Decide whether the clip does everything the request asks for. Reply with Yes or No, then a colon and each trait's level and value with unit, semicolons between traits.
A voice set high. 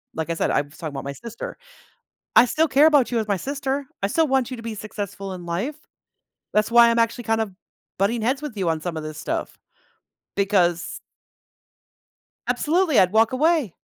Yes: high, 225 Hz